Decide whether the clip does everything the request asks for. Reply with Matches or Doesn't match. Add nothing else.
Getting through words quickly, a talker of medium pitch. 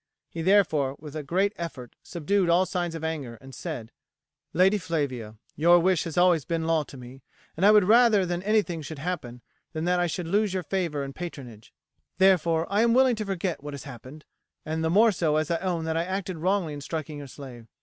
Matches